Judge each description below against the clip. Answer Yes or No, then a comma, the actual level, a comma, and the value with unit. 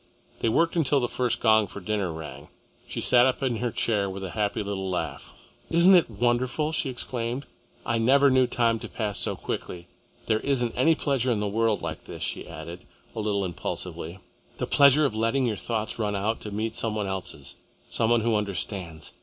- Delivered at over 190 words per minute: Yes, average, 200 wpm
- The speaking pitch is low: Yes, low, 115 Hz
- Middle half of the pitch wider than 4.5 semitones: No, average, 3.8 semitones